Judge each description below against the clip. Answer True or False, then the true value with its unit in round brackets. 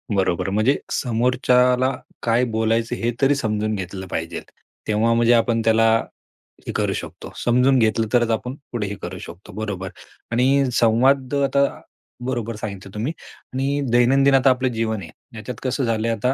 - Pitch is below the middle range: True (115 Hz)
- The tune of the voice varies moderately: True (3.0 semitones)